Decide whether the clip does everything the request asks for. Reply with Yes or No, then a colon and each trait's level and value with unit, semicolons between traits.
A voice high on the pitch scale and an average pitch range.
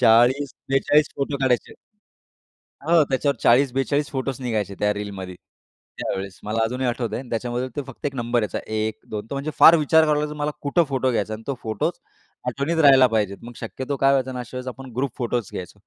No: low, 130 Hz; average, 3.6 semitones